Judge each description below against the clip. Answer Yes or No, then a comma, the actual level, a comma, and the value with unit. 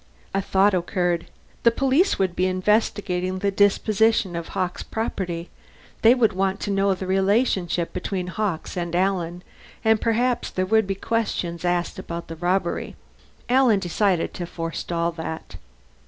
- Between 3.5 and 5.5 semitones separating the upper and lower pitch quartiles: No, average, 3.0 semitones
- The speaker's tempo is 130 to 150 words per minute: Yes, average, 145 wpm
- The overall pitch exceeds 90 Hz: Yes, high, 190 Hz